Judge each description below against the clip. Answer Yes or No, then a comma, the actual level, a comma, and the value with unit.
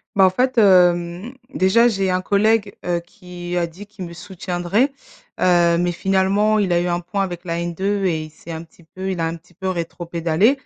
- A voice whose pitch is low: No, medium, 180 Hz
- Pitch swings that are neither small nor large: No, narrow, 2.3 semitones